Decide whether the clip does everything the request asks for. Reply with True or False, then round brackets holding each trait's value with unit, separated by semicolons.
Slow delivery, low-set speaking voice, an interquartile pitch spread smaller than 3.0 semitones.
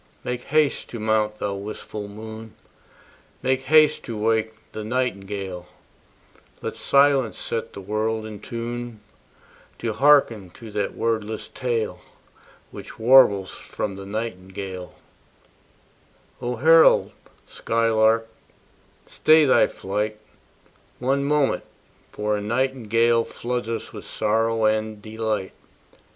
True (110 wpm; 110 Hz; 2.5 semitones)